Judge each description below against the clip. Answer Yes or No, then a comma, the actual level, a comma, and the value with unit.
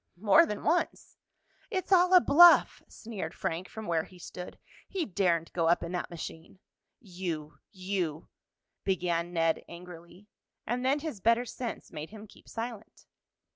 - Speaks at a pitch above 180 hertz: Yes, high, 190 Hz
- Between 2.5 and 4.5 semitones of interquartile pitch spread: No, wide, 5.6 semitones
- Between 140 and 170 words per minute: Yes, average, 155 wpm